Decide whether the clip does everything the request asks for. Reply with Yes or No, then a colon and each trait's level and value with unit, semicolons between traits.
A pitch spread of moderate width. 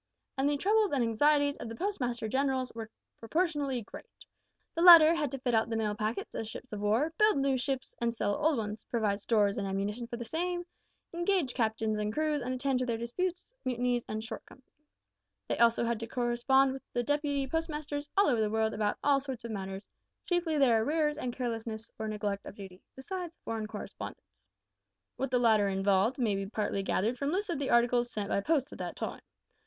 Yes: average, 4.8 semitones